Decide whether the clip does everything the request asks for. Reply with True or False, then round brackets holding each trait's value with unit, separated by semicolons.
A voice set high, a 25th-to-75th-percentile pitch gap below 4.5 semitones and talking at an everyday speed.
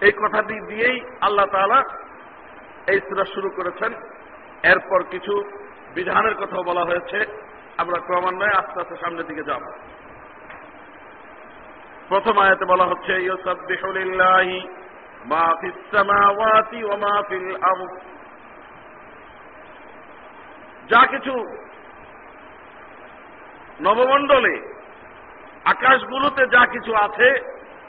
True (195 Hz; 3.1 semitones; 70 wpm)